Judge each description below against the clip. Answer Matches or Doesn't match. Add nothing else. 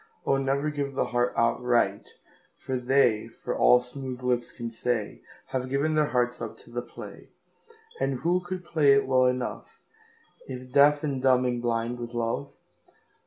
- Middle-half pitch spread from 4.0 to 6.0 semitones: Doesn't match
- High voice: Doesn't match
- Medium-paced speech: Matches